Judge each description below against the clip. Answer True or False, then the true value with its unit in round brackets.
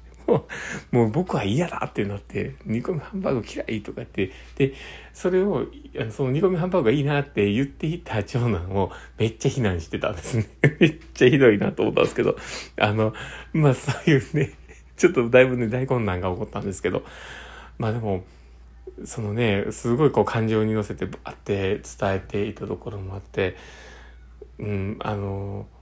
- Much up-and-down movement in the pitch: False (4.9 semitones)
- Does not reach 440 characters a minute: True (350 characters per minute)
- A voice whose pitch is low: True (110 Hz)